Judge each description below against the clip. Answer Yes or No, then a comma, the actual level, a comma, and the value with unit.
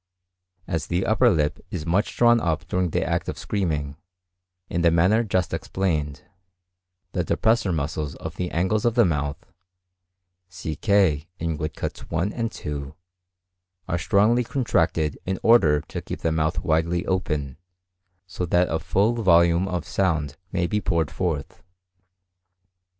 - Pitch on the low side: Yes, very low, 85 Hz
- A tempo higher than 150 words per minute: No, average, 145 wpm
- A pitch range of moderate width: Yes, average, 3.8 semitones